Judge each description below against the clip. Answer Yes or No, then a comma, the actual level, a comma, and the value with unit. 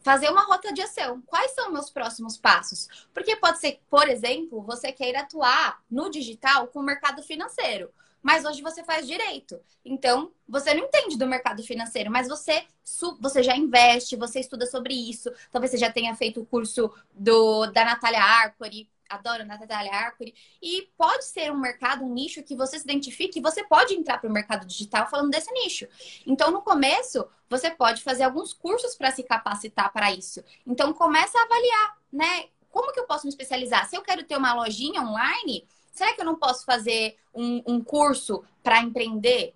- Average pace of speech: No, fast, 190 wpm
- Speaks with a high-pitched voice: Yes, very high, 265 Hz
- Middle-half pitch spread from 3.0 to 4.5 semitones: No, average, 5.1 semitones